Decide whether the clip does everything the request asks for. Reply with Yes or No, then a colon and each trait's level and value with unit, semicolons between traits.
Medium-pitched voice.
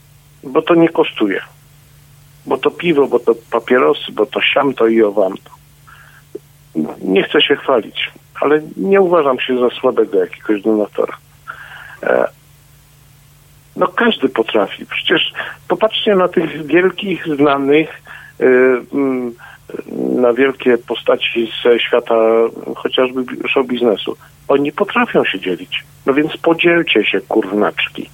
Yes: medium, 145 Hz